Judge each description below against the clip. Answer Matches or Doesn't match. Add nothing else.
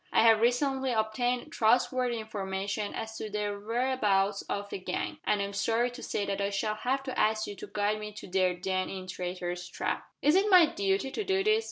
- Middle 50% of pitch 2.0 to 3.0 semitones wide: Doesn't match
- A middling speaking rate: Doesn't match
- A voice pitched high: Matches